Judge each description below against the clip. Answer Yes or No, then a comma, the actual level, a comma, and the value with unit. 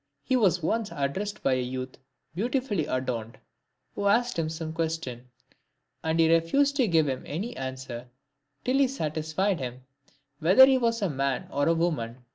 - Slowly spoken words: No, average, 165 wpm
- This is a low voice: No, medium, 160 Hz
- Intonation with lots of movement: Yes, wide, 7.8 semitones